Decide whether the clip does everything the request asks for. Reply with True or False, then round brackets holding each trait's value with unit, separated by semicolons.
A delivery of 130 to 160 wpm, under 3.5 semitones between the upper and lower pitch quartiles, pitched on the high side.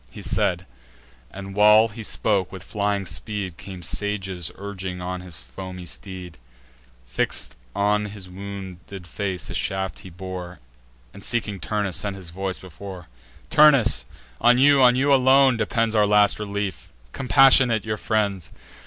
False (145 wpm; 2.7 semitones; 100 Hz)